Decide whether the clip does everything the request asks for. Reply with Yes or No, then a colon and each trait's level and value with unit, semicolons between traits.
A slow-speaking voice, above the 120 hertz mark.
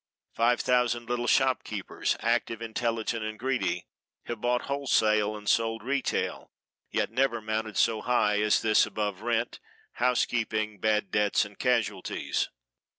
No: slow, 130 wpm; low, 115 Hz